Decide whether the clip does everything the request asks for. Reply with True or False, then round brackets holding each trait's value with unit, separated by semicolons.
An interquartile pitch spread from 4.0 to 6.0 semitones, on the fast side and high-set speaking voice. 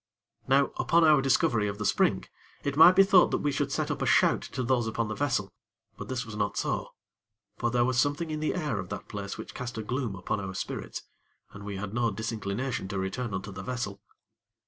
False (5.1 semitones; 225 wpm; 120 Hz)